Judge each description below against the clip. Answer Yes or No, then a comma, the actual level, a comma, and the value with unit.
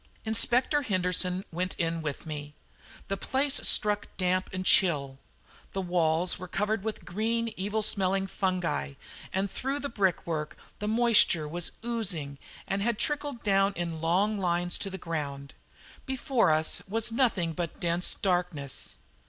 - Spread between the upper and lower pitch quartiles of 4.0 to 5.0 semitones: Yes, average, 4.5 semitones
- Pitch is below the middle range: No, medium, 185 Hz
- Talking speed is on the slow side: No, average, 145 wpm